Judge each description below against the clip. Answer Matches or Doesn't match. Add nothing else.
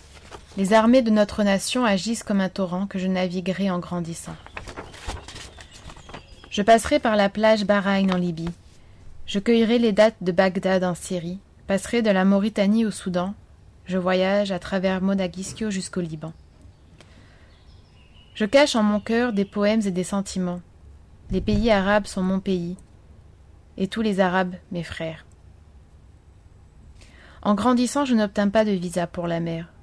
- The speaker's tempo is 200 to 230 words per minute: Doesn't match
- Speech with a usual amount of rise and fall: Matches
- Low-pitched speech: Doesn't match